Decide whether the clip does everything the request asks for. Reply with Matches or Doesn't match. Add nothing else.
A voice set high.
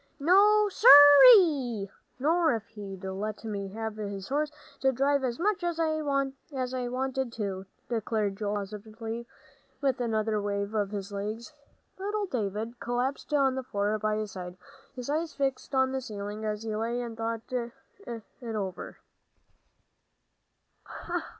Matches